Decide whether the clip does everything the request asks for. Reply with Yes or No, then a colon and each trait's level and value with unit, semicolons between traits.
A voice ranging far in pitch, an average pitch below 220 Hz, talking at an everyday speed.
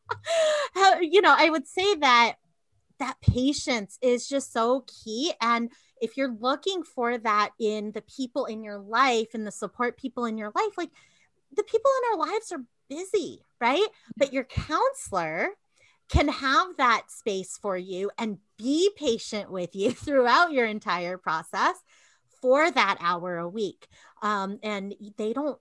No: wide, 7.2 semitones; high, 245 Hz; average, 155 wpm